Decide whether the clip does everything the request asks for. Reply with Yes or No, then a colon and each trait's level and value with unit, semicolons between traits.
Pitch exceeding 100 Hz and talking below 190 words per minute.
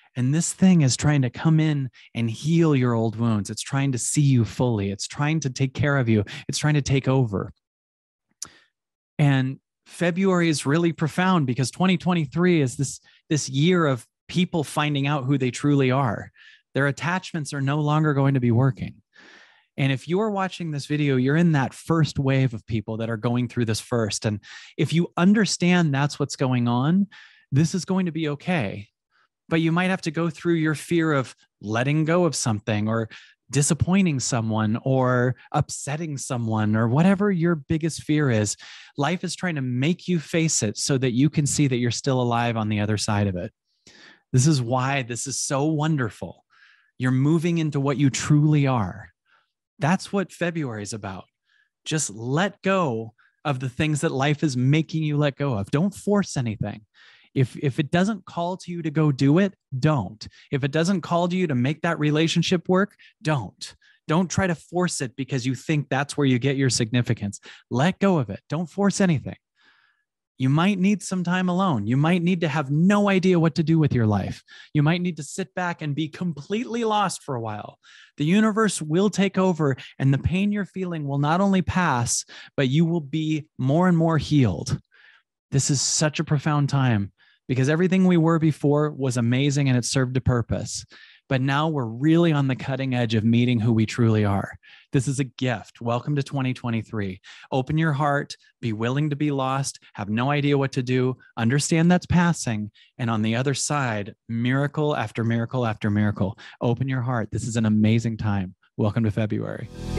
No: medium, 140 Hz; average, 195 wpm